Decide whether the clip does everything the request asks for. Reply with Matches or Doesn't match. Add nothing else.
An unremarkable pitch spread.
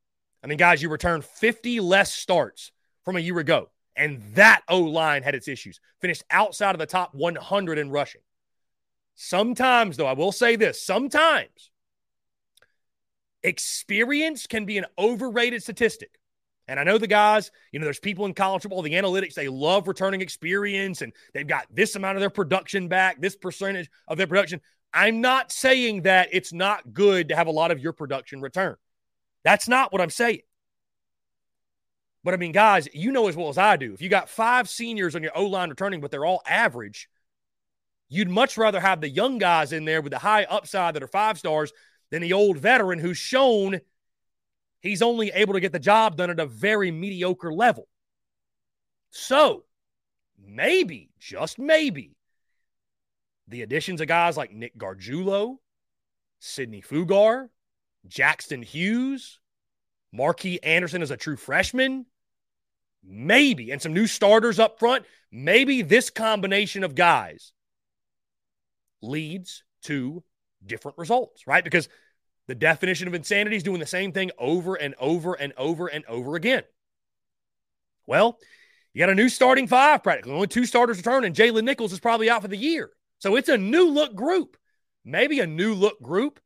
Doesn't match